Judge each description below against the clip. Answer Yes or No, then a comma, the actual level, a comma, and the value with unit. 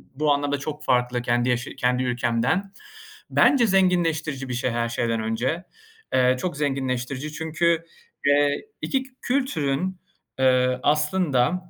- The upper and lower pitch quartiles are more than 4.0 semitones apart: Yes, average, 4.7 semitones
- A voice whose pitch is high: No, medium, 140 Hz